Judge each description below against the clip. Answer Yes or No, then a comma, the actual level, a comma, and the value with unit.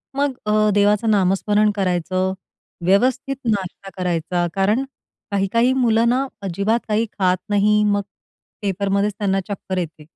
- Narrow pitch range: Yes, narrow, 2.3 semitones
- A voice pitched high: Yes, high, 200 Hz